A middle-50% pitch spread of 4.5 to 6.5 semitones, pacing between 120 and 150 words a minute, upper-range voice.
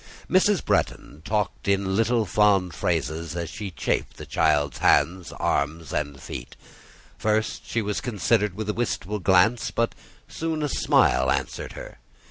No: average, 5.2 semitones; average, 145 wpm; low, 100 Hz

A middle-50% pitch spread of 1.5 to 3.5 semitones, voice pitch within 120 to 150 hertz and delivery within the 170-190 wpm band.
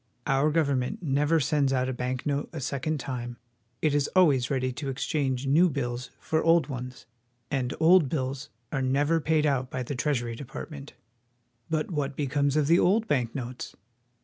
Yes: average, 3.0 semitones; medium, 140 Hz; average, 175 wpm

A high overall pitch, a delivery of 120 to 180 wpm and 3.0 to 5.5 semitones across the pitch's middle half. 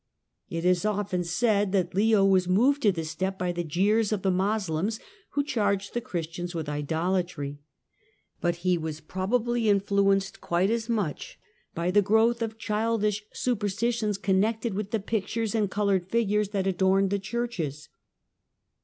Yes: high, 200 Hz; average, 155 wpm; average, 3.4 semitones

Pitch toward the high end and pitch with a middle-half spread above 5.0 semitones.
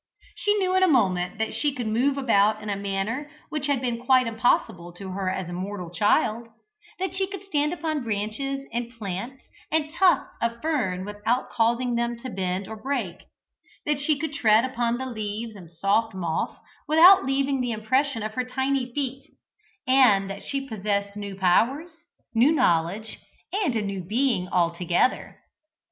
Yes: high, 235 Hz; wide, 5.5 semitones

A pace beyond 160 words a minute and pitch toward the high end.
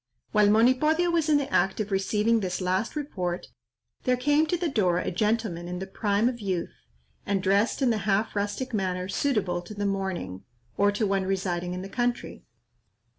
Yes: average, 185 wpm; high, 205 Hz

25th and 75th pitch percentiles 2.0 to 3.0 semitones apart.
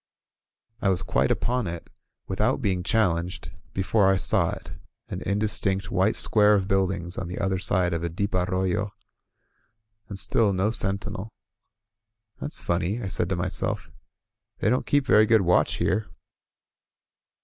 Yes: narrow, 2.5 semitones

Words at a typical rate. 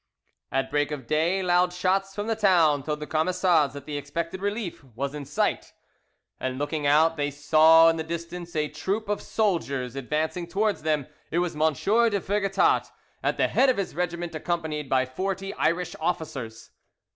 Yes: average, 175 wpm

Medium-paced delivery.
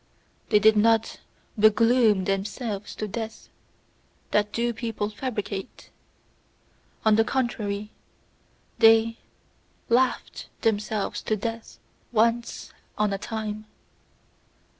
No: slow, 95 wpm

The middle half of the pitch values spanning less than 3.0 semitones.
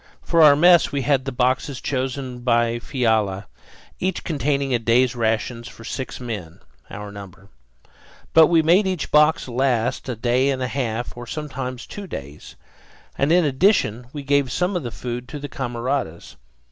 No: average, 3.6 semitones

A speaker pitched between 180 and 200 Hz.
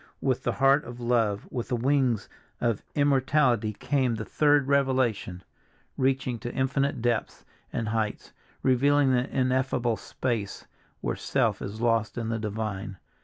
No: low, 125 Hz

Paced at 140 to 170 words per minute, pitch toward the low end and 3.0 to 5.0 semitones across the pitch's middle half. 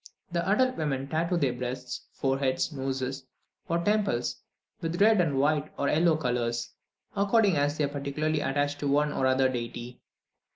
No: average, 160 wpm; medium, 145 Hz; average, 4.1 semitones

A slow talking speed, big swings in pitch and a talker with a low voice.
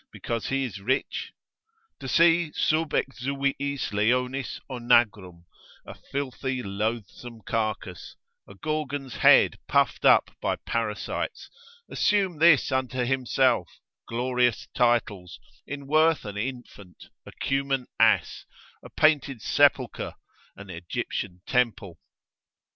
No: slow, 105 wpm; average, 4.0 semitones; low, 125 Hz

